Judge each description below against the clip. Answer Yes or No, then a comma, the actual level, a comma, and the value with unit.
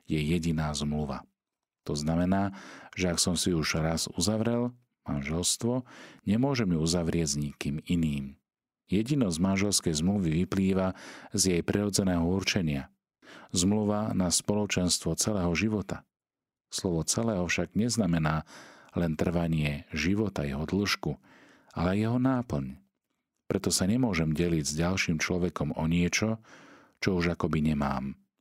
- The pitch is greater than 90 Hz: No, very low, 85 Hz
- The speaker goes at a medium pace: Yes, average, 120 wpm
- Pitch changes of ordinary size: Yes, average, 4.0 semitones